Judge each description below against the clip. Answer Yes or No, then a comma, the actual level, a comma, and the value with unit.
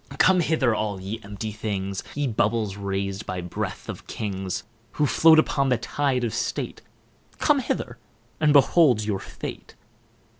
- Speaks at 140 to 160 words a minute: Yes, average, 150 wpm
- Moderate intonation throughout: No, wide, 5.9 semitones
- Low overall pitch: Yes, low, 110 Hz